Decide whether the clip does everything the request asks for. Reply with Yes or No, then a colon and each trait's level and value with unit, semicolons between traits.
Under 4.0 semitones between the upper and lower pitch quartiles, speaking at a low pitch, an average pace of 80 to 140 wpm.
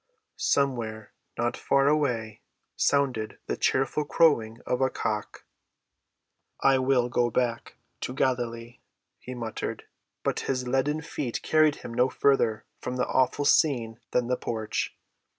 Yes: average, 2.8 semitones; low, 125 Hz; slow, 135 wpm